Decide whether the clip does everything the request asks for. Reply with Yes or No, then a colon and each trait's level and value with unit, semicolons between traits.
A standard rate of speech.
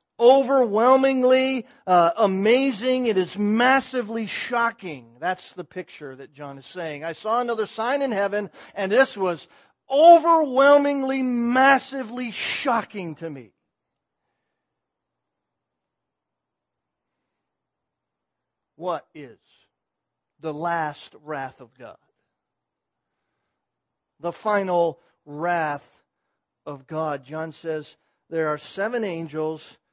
No: slow, 90 wpm